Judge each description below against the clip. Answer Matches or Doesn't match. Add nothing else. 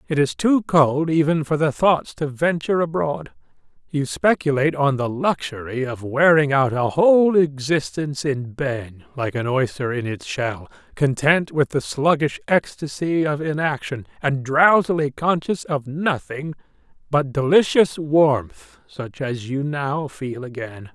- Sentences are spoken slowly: Doesn't match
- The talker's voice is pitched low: Doesn't match